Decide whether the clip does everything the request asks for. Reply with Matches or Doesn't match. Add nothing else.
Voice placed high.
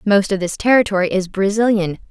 Matches